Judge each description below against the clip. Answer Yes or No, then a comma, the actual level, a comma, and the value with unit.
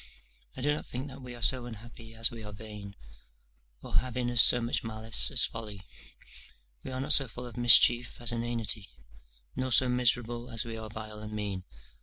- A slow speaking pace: No, average, 200 wpm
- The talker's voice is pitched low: Yes, low, 120 Hz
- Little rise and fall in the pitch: Yes, narrow, 2.1 semitones